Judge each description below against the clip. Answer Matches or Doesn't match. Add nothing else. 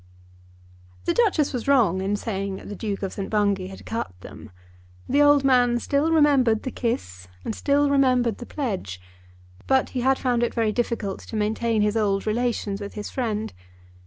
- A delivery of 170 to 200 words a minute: Matches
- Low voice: Doesn't match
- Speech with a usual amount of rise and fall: Matches